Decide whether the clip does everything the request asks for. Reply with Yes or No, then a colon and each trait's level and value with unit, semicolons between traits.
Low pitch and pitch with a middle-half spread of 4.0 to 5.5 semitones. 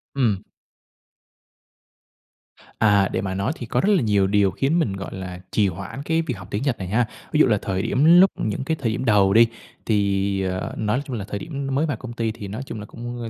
Yes: low, 110 Hz; average, 4.9 semitones